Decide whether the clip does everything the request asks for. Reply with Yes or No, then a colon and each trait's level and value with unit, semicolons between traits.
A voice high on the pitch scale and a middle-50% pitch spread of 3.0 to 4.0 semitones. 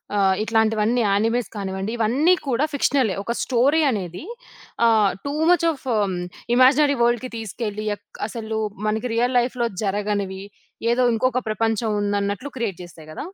Yes: high, 225 Hz; average, 3.5 semitones